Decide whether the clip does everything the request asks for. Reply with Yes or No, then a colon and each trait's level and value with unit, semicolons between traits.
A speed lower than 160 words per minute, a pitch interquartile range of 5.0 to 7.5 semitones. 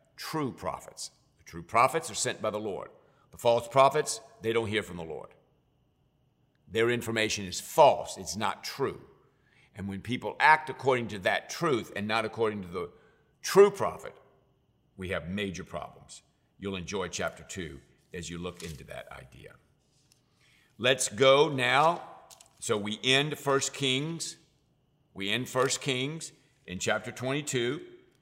Yes: average, 150 wpm; average, 5.3 semitones